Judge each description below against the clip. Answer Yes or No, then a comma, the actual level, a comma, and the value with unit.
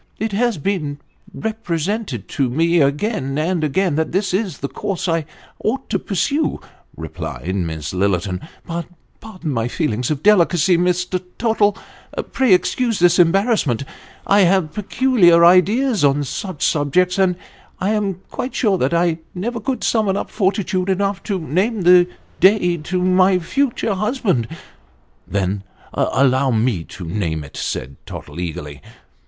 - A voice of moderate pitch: Yes, medium, 180 Hz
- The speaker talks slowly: No, average, 150 wpm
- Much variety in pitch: Yes, wide, 6.5 semitones